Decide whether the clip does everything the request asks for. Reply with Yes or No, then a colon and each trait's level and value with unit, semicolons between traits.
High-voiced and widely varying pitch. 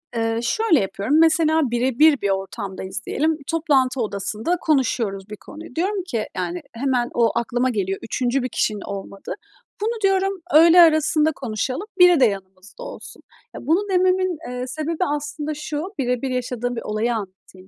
Yes: very high, 255 Hz; wide, 6.9 semitones